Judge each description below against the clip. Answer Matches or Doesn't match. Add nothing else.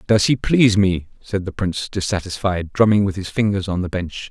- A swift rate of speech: Matches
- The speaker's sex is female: Doesn't match